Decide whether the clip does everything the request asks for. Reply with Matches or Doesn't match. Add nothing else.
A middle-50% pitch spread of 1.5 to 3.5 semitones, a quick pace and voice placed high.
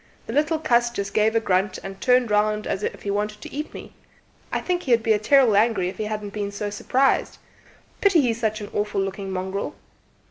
Matches